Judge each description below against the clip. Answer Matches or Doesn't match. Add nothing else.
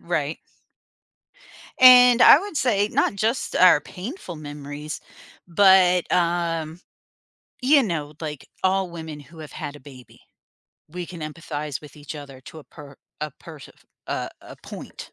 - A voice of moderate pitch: Matches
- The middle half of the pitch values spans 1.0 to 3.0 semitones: Doesn't match